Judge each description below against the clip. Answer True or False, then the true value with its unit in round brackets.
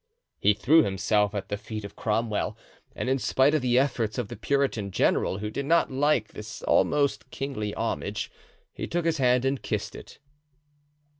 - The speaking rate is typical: True (175 wpm)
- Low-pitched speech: True (125 Hz)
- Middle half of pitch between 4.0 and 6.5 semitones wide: True (4.8 semitones)